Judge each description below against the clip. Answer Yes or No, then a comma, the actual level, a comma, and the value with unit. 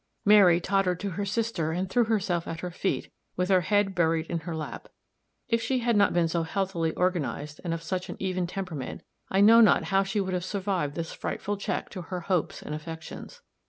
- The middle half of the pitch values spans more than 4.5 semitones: No, average, 3.1 semitones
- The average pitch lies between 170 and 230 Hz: Yes, medium, 185 Hz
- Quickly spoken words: Yes, fast, 210 wpm